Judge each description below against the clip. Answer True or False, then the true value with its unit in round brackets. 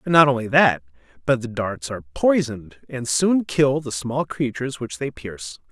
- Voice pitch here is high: False (125 Hz)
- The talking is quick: False (180 wpm)